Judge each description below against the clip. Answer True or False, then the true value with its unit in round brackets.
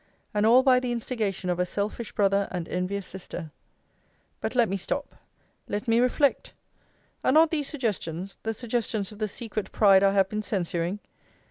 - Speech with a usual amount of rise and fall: True (3.7 semitones)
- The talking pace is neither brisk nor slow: True (170 wpm)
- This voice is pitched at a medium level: False (210 Hz)